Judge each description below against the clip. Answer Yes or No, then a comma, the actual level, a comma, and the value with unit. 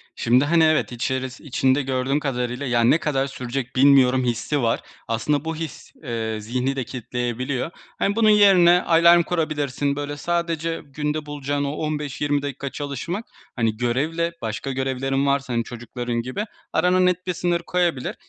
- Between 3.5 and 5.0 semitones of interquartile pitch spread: Yes, average, 4.2 semitones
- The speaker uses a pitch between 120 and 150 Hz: Yes, medium, 140 Hz